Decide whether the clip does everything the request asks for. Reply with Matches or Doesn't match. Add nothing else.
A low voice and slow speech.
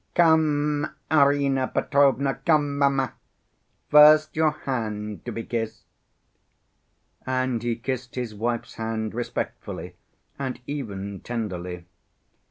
Matches